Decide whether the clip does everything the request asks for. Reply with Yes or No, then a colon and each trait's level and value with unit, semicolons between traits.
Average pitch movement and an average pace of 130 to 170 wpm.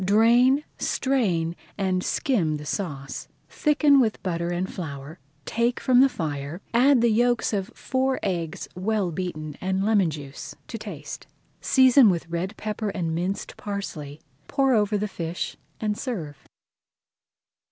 No: wide, 6.1 semitones; average, 140 wpm